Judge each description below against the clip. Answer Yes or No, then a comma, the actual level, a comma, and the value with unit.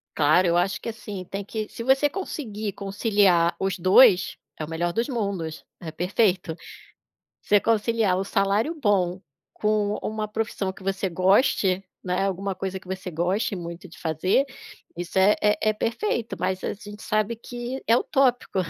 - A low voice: No, high, 195 Hz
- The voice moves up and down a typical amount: Yes, average, 3.0 semitones